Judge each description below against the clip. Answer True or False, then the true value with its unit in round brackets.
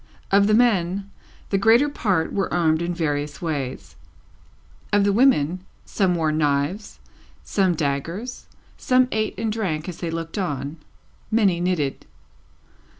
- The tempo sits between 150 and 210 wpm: False (135 wpm)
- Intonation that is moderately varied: True (4.8 semitones)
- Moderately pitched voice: True (180 Hz)